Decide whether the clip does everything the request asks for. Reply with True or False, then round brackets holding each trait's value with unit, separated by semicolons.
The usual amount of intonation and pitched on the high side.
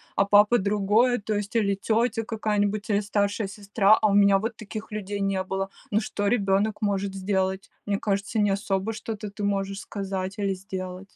False (1.5 semitones; 200 Hz)